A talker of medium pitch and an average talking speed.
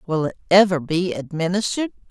Yes: medium, 180 Hz; average, 145 wpm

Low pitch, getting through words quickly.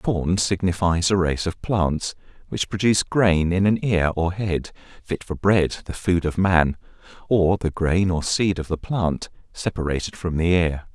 No: very low, 90 Hz; average, 180 wpm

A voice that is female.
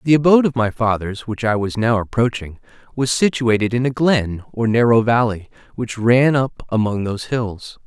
No: male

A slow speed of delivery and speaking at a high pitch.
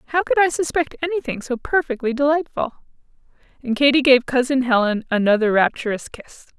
No: average, 145 wpm; very high, 265 Hz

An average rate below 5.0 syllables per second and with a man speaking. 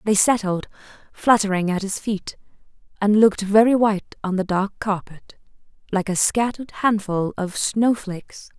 No: 4.8 syllables/s; female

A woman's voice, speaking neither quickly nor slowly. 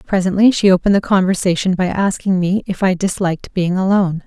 Yes: female; average, 185 wpm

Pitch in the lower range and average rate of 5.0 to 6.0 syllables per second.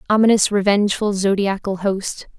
No: high, 200 Hz; 5.2 syllables/s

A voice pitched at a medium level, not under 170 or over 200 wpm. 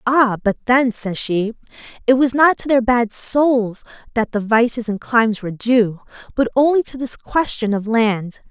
No: high, 235 Hz; average, 185 wpm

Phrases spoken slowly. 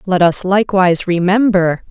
Yes: slow, 125 wpm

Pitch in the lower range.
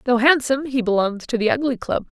No: high, 245 Hz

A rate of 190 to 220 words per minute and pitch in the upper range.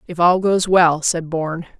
No: average, 200 wpm; medium, 170 Hz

